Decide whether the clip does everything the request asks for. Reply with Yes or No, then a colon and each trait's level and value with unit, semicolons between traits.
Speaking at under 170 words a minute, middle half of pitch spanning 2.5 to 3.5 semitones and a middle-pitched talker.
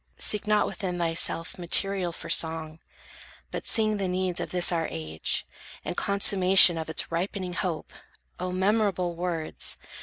Yes: average, 145 wpm; average, 2.8 semitones; medium, 180 Hz